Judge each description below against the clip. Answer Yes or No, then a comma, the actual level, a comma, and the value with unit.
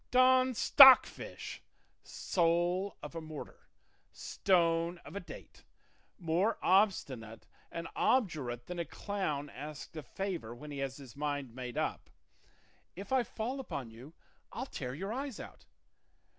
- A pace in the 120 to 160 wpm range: Yes, slow, 135 wpm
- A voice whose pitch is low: No, medium, 170 Hz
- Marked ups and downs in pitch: Yes, wide, 6.2 semitones